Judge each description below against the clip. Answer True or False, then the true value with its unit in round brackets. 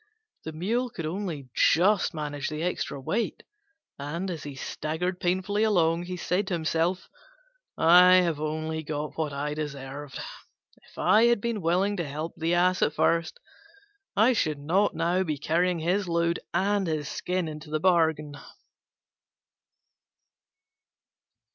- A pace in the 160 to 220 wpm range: False (140 wpm)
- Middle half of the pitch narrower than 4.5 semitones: True (3.1 semitones)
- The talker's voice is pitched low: False (170 Hz)